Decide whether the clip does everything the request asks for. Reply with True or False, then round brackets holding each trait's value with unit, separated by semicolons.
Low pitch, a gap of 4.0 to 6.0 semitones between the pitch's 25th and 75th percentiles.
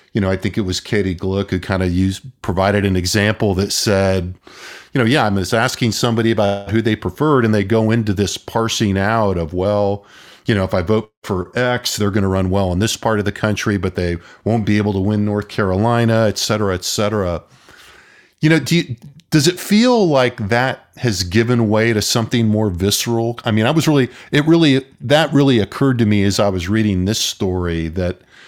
False (110 Hz; 3.3 semitones)